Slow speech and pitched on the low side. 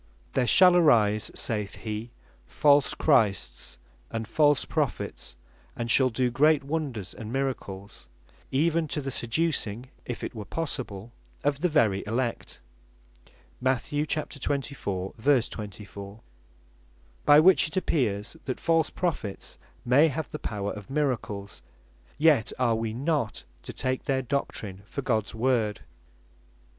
Yes: slow, 125 wpm; low, 125 Hz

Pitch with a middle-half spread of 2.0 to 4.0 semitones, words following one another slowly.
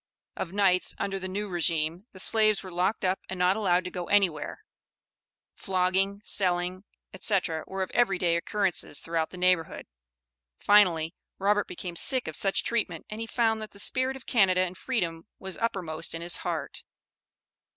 No: average, 2.7 semitones; average, 170 wpm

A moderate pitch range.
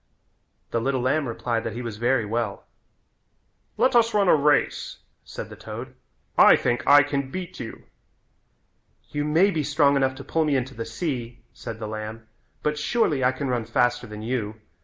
Yes: average, 4.3 semitones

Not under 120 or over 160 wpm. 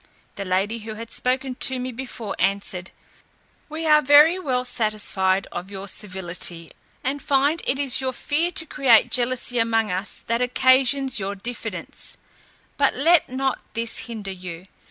Yes: average, 155 wpm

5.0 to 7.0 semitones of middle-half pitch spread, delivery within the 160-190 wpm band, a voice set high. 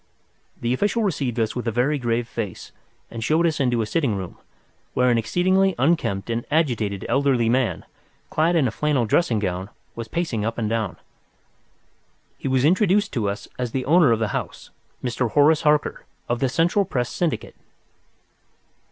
No: wide, 5.4 semitones; average, 170 wpm; low, 125 Hz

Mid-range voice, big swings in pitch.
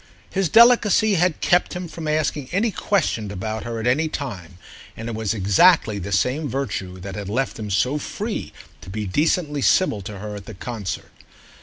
No: low, 120 Hz; wide, 8.1 semitones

